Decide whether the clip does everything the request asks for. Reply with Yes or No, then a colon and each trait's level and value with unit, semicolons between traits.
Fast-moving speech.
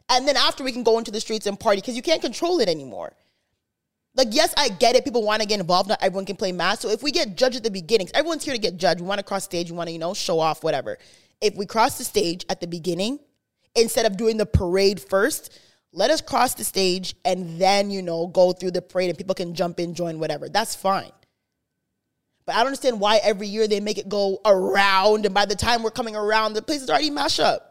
Yes: fast, 260 wpm